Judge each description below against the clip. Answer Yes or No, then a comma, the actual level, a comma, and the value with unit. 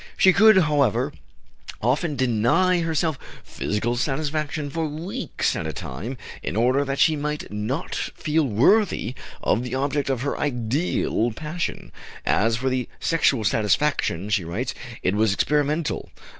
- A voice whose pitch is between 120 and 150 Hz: Yes, low, 135 Hz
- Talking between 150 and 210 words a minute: No, average, 140 wpm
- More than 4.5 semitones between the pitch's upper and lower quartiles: Yes, average, 5.0 semitones